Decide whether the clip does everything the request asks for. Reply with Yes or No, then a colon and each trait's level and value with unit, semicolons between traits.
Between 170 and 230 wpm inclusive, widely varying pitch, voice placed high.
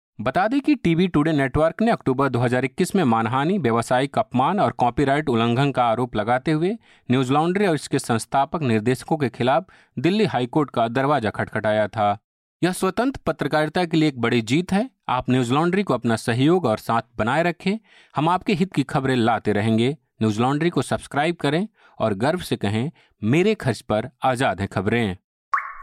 No: average, 175 wpm; wide, 6.3 semitones; low, 135 Hz